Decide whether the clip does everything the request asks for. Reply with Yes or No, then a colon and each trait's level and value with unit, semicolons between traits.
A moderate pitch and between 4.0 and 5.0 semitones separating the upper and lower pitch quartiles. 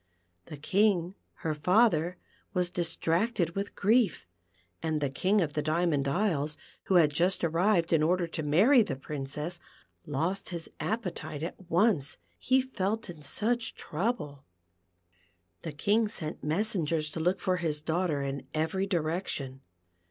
Yes: medium, 170 Hz; average, 4.5 semitones